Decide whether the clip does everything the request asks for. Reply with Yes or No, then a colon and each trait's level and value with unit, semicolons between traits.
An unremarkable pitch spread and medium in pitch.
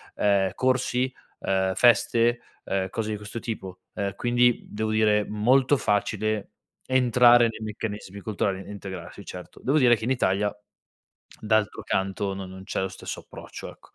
No: average, 3.5 semitones; low, 105 Hz